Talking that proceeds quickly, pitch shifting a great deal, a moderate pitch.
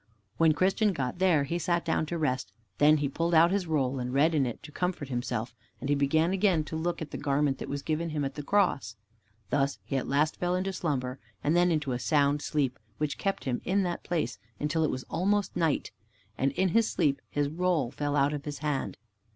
No: fast, 230 wpm; average, 3.7 semitones; medium, 150 Hz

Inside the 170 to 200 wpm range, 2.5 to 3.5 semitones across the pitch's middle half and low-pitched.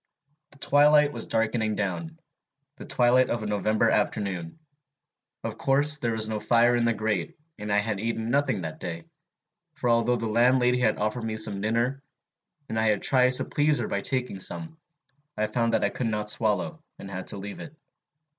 Yes: average, 185 wpm; average, 3.2 semitones; low, 115 Hz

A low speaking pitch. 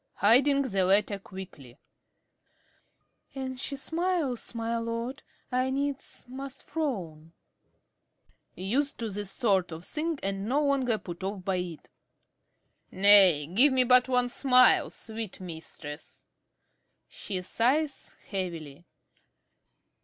No: high, 225 Hz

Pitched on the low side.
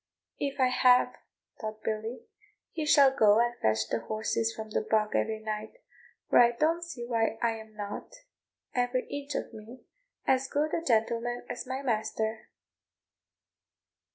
No: high, 235 Hz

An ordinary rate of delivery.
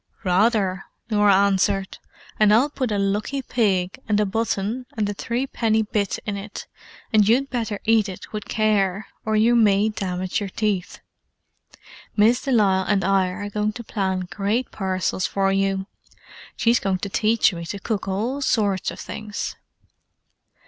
Yes: average, 160 wpm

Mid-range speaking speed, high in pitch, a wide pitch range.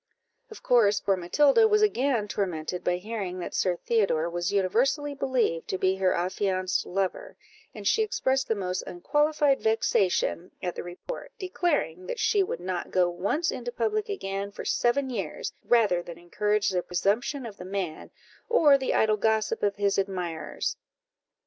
Yes: average, 160 wpm; high, 205 Hz; wide, 6.8 semitones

